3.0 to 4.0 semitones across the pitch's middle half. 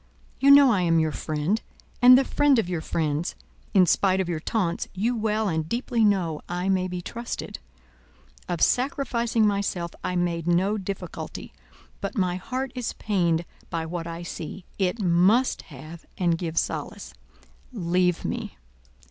No: average, 4.6 semitones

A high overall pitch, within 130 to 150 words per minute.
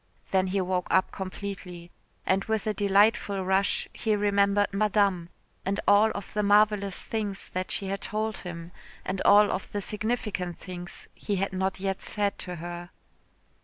No: high, 195 Hz; average, 165 wpm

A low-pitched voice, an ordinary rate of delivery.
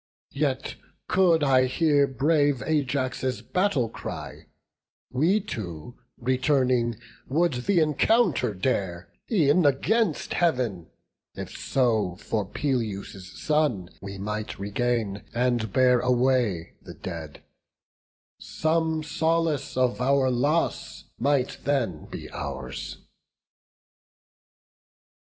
No: low, 130 Hz; slow, 95 wpm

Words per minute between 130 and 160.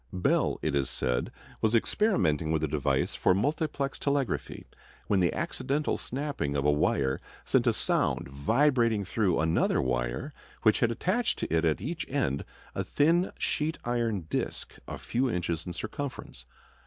Yes: average, 155 wpm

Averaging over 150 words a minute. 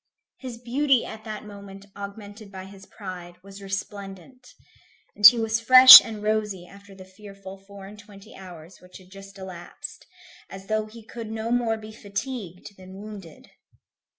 Yes: average, 160 wpm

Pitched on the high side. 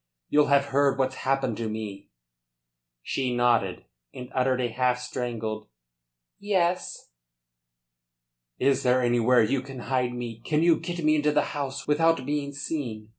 No: low, 130 Hz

